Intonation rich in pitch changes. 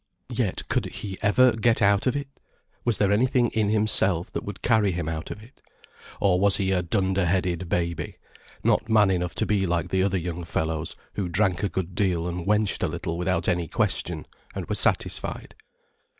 No: average, 3.2 semitones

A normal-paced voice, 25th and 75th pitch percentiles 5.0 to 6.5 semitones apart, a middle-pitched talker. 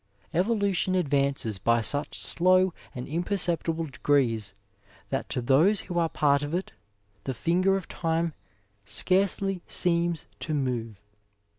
No: slow, 125 wpm; average, 5.3 semitones; medium, 165 Hz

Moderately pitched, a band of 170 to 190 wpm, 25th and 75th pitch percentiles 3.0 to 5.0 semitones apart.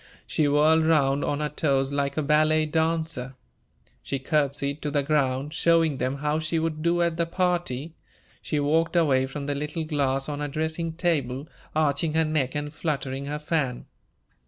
No: medium, 150 Hz; average, 175 wpm; narrow, 2.4 semitones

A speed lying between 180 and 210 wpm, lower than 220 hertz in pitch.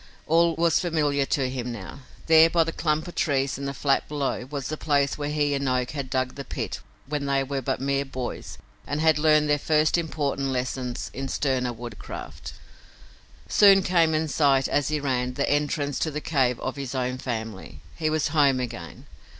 Yes: average, 195 wpm; medium, 140 Hz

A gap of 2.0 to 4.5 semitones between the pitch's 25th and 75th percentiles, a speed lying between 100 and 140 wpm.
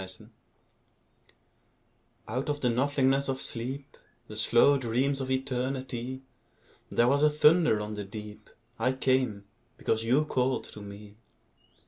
Yes: average, 3.5 semitones; slow, 135 wpm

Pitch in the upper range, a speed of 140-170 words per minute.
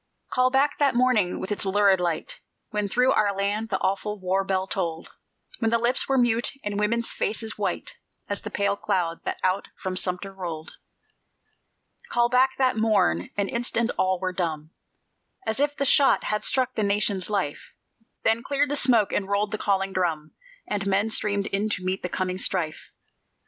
No: high, 205 Hz; average, 180 wpm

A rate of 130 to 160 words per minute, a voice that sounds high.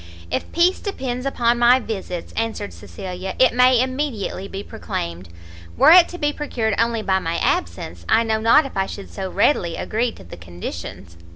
No: average, 180 wpm; high, 225 Hz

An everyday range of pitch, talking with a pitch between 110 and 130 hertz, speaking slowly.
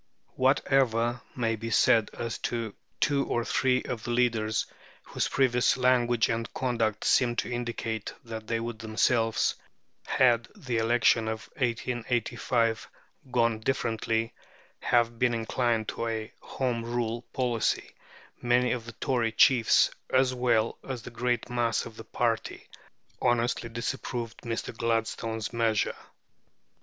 No: narrow, 1.4 semitones; low, 115 Hz; slow, 130 wpm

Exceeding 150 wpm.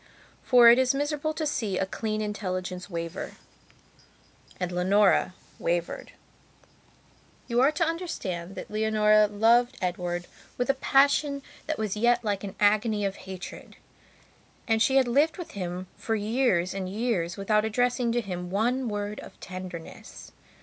No: average, 145 wpm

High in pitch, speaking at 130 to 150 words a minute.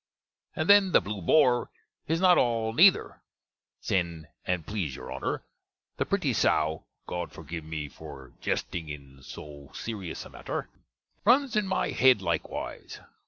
No: very low, 90 Hz; average, 145 wpm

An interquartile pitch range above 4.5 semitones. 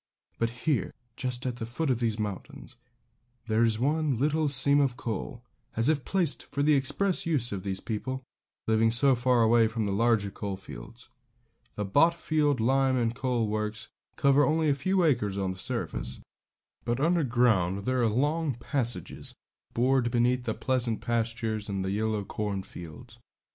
No: average, 4.0 semitones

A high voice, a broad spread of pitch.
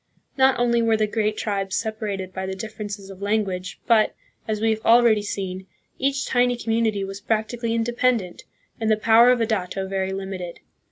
No: high, 215 Hz; average, 2.9 semitones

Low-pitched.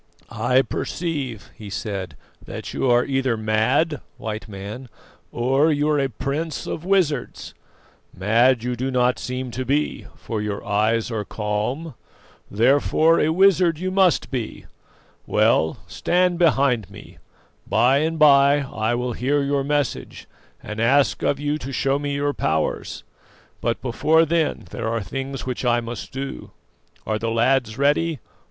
Yes: low, 130 Hz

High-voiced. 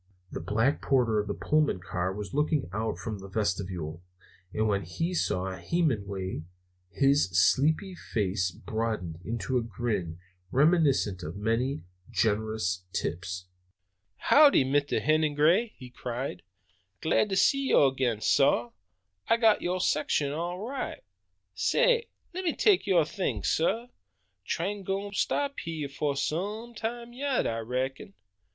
No: low, 135 Hz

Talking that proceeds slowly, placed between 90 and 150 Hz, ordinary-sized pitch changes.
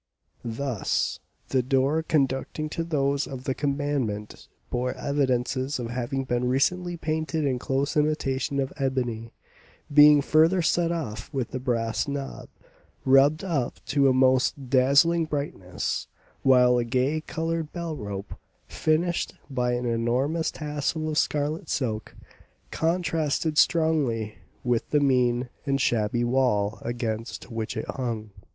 Yes: slow, 130 wpm; low, 135 Hz; average, 3.8 semitones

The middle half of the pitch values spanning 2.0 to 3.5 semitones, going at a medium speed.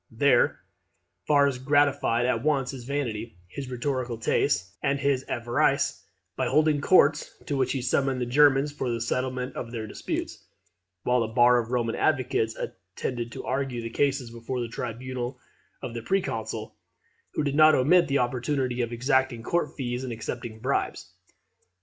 Yes: average, 2.8 semitones; average, 160 wpm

